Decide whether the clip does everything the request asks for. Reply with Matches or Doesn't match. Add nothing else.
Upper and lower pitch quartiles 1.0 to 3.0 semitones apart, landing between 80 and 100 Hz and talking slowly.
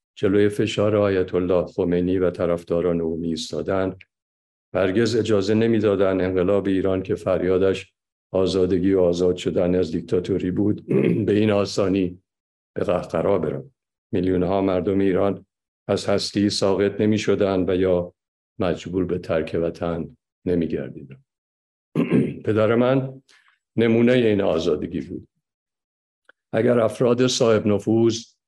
Matches